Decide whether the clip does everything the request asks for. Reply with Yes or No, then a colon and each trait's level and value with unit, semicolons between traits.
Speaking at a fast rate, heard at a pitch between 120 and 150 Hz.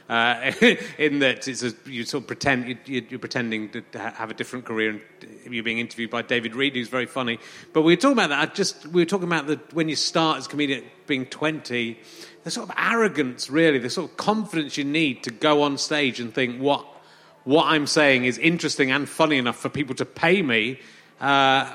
Yes: fast, 225 wpm; low, 135 Hz